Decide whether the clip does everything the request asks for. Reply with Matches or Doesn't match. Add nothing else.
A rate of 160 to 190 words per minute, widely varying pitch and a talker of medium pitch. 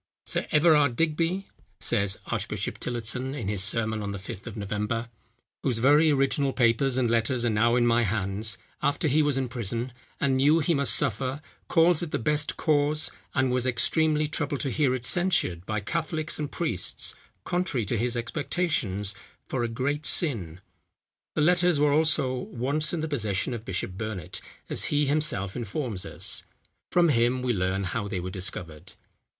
Doesn't match